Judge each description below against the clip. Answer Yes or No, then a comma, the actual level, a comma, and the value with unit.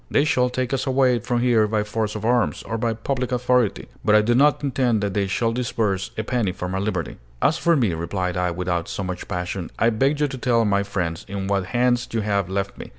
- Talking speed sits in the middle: No, fast, 240 wpm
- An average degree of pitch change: Yes, average, 4.3 semitones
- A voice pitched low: Yes, low, 110 Hz